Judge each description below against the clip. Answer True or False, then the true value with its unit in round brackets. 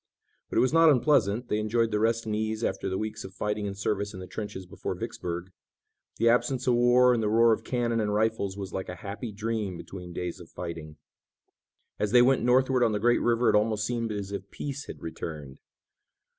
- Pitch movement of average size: True (3.4 semitones)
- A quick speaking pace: True (215 wpm)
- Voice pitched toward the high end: False (110 Hz)